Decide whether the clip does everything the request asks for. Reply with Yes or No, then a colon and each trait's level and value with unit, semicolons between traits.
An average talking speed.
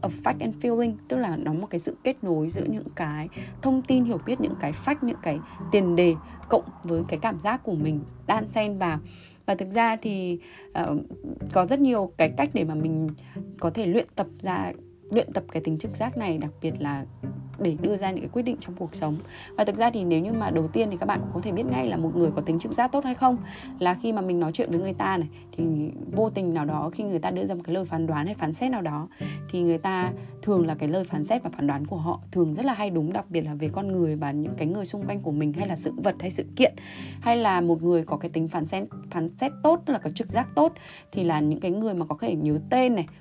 No: fast, 275 wpm